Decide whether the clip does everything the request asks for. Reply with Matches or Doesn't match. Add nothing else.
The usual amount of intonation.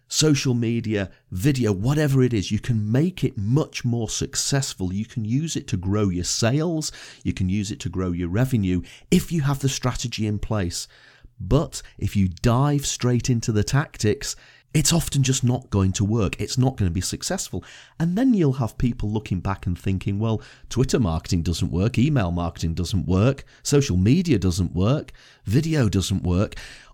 Doesn't match